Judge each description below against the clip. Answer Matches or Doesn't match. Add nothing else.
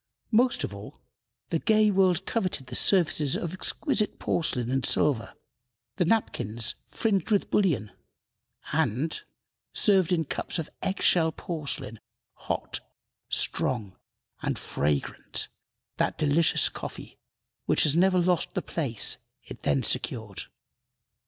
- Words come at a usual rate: Doesn't match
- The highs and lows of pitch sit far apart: Matches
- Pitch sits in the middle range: Matches